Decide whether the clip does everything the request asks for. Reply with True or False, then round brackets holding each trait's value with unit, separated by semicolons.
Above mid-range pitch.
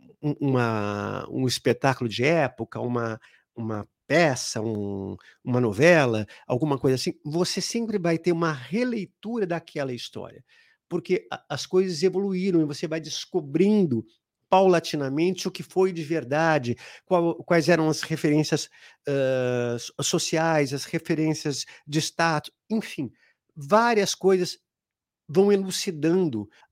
False (160 Hz)